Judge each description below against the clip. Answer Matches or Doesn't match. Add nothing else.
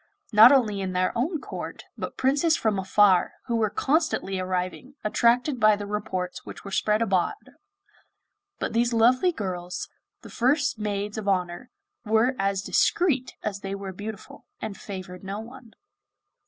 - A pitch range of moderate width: Matches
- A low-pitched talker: Doesn't match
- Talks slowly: Doesn't match